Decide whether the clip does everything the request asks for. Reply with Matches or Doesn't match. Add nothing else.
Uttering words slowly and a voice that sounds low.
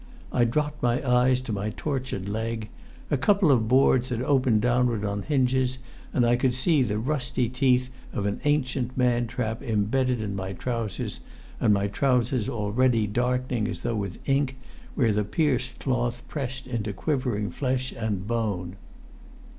Doesn't match